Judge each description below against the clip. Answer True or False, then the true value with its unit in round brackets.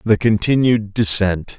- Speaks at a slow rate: True (115 wpm)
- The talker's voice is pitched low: True (105 Hz)